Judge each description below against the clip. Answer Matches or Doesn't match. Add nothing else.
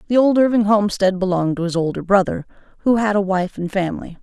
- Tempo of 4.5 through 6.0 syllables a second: Doesn't match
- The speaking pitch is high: Matches